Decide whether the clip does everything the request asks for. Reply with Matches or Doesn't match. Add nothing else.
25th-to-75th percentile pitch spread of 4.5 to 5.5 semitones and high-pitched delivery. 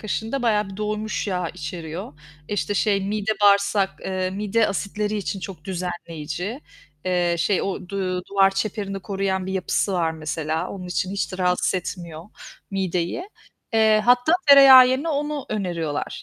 Doesn't match